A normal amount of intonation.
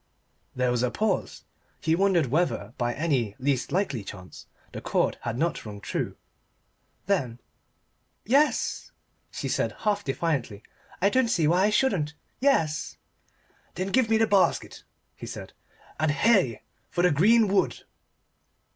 No: wide, 8.1 semitones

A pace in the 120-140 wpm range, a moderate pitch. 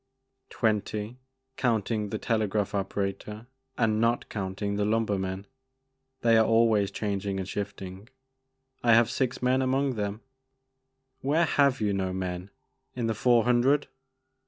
No: slow, 135 wpm; low, 110 Hz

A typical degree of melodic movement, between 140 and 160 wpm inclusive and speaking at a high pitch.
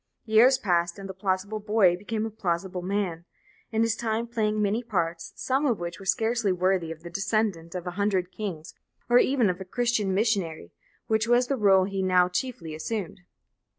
No: average, 3.7 semitones; average, 190 wpm; high, 200 Hz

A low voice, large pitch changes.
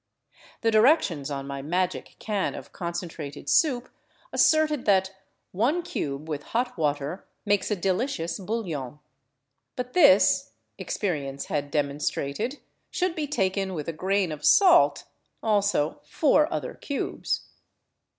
No: high, 190 Hz; wide, 8.6 semitones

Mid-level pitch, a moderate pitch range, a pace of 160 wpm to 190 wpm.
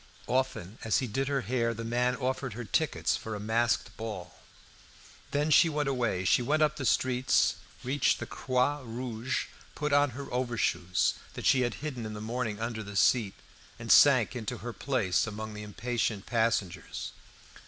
No: low, 120 Hz; average, 3.1 semitones; average, 175 wpm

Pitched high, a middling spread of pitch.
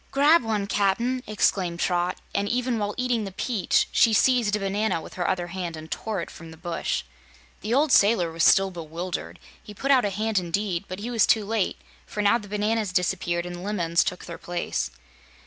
Yes: high, 200 Hz; average, 3.9 semitones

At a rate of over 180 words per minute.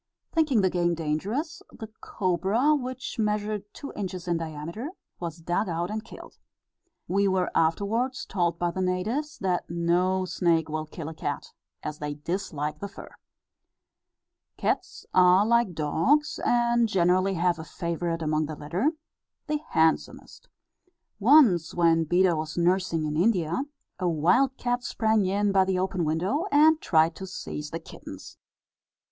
No: average, 150 wpm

